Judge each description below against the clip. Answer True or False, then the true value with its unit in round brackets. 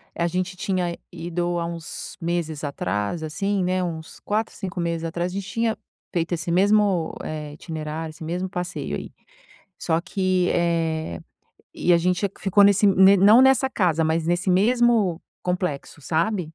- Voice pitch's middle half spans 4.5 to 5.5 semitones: False (2.8 semitones)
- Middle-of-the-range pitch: True (175 Hz)